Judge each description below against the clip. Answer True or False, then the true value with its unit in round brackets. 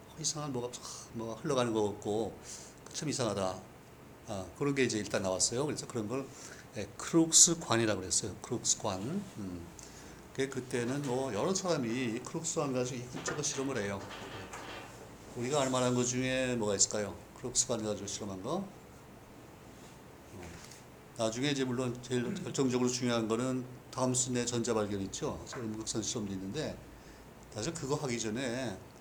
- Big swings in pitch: False (4.0 semitones)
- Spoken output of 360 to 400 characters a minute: False (320 characters per minute)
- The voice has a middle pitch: False (125 Hz)